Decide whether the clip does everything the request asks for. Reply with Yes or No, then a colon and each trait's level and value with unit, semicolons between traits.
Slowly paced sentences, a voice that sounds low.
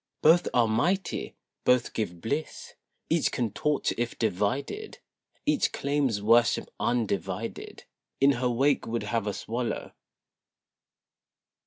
Yes: slow, 115 wpm; low, 120 Hz